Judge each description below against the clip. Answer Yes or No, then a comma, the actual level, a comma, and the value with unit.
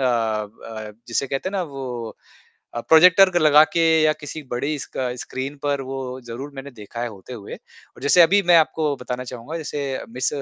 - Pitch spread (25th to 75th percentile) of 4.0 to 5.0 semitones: Yes, average, 4.4 semitones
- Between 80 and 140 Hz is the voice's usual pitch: Yes, low, 135 Hz